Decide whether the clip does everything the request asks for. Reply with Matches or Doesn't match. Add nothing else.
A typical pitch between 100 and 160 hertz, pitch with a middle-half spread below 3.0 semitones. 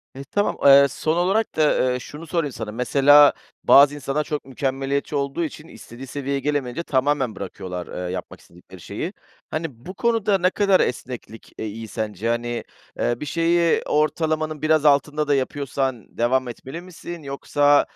Doesn't match